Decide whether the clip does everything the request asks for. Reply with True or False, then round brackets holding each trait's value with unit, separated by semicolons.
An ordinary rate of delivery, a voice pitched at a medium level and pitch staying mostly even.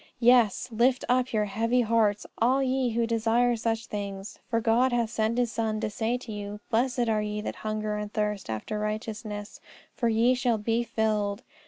False (185 wpm; 225 Hz; 2.1 semitones)